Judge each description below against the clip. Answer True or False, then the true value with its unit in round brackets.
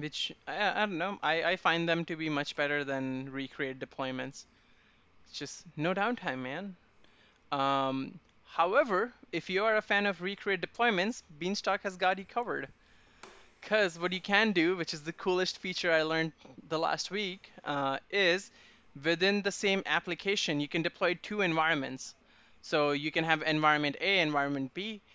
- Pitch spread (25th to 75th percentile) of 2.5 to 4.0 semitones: False (4.9 semitones)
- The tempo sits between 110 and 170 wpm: True (165 wpm)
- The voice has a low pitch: False (170 Hz)